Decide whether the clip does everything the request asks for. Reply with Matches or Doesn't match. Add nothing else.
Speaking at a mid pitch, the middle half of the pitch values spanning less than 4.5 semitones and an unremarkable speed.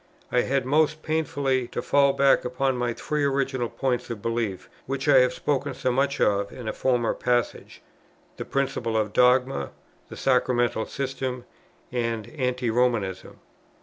Doesn't match